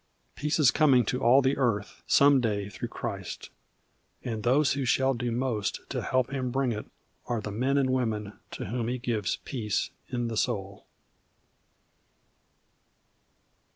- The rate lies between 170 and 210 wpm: No, average, 155 wpm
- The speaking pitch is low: Yes, low, 125 Hz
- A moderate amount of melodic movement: Yes, average, 3.4 semitones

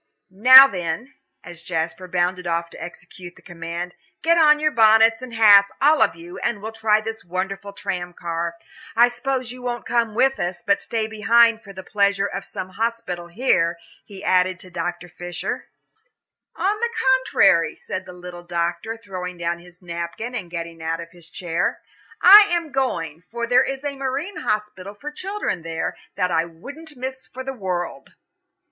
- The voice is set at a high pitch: Yes, high, 195 Hz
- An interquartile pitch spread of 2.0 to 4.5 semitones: No, wide, 5.6 semitones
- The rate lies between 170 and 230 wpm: Yes, average, 180 wpm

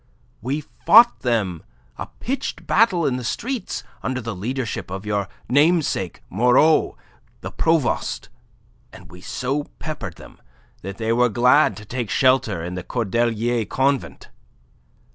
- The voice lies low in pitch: Yes, low, 125 Hz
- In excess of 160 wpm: No, slow, 135 wpm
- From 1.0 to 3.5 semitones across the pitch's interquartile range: No, wide, 5.4 semitones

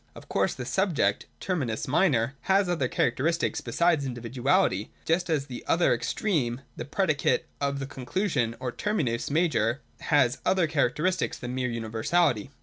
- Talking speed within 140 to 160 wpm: Yes, average, 145 wpm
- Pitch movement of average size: No, wide, 5.9 semitones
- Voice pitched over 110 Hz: Yes, medium, 140 Hz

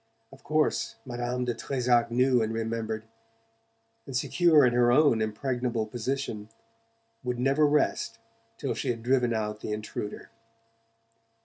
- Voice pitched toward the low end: Yes, low, 120 Hz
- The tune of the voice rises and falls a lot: No, average, 2.8 semitones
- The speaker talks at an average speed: No, slow, 130 wpm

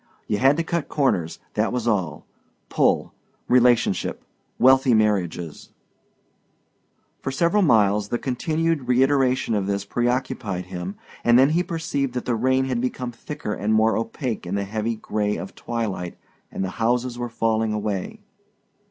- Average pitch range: Yes, average, 4.1 semitones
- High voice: No, low, 120 Hz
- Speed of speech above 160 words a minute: No, average, 150 wpm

